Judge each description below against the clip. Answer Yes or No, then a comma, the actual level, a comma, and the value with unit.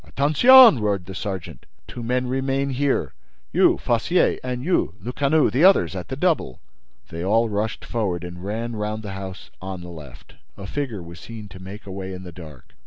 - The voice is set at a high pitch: No, low, 105 Hz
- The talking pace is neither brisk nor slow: Yes, average, 175 wpm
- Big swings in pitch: Yes, wide, 6.0 semitones